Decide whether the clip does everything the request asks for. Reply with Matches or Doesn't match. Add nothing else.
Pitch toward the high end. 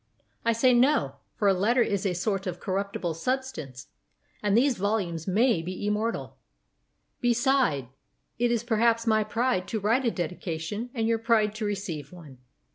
Matches